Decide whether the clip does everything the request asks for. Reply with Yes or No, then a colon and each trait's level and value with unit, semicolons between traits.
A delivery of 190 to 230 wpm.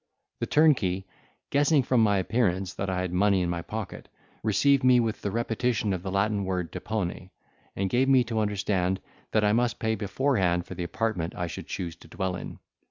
Yes: average, 195 wpm